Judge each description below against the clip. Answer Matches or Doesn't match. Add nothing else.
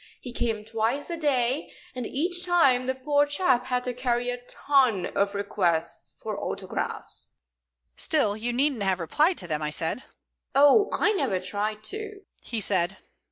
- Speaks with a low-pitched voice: Doesn't match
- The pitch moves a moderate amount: Doesn't match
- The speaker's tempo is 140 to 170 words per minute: Matches